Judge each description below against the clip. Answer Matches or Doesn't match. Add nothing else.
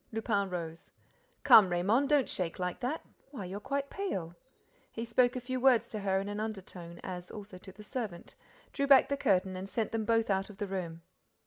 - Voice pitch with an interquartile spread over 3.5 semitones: Matches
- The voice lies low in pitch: Doesn't match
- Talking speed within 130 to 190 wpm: Doesn't match